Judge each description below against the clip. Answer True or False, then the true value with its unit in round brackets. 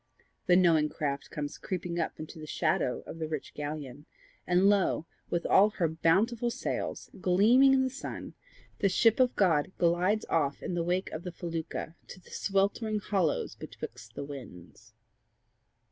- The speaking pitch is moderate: True (175 Hz)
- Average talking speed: True (160 wpm)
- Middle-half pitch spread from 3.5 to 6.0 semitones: True (4.4 semitones)